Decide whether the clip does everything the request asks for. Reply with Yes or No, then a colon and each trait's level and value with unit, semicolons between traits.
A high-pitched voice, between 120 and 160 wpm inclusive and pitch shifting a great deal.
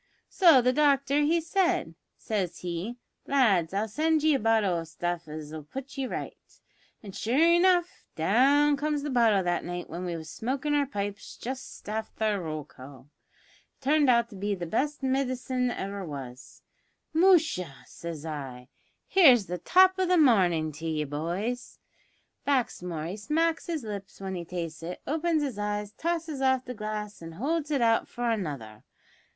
No: high, 220 Hz; average, 170 wpm; wide, 8.6 semitones